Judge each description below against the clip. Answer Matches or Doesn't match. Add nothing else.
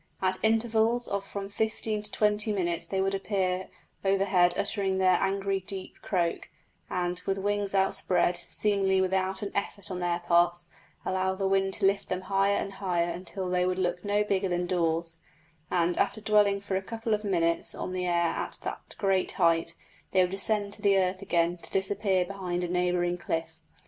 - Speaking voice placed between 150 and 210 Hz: Matches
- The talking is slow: Doesn't match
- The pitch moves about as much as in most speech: Doesn't match